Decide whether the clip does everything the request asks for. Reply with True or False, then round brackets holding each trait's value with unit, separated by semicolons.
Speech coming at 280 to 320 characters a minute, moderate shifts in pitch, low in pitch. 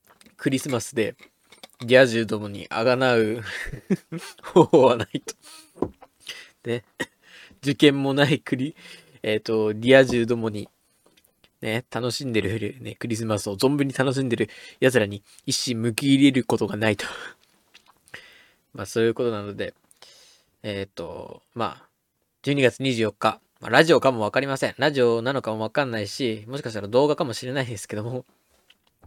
True (295 characters per minute; 3.7 semitones; 120 Hz)